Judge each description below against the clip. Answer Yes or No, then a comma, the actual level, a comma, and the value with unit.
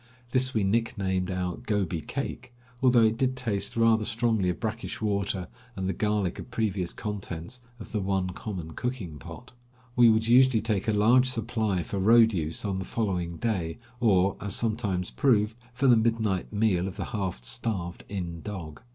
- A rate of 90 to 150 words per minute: No, average, 175 wpm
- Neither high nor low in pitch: No, low, 105 Hz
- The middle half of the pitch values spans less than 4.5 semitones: Yes, average, 3.7 semitones